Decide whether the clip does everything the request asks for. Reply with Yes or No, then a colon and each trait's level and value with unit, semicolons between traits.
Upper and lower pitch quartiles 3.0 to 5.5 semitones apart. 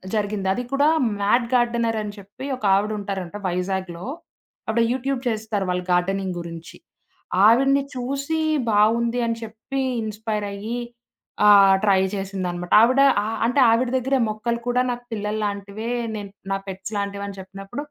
Yes: average, 3.3 semitones